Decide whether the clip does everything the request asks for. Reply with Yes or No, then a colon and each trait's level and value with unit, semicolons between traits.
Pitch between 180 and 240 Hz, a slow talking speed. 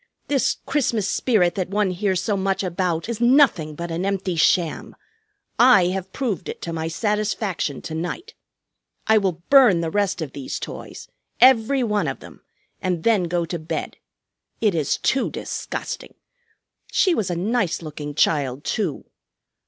No: high, 190 Hz; average, 160 wpm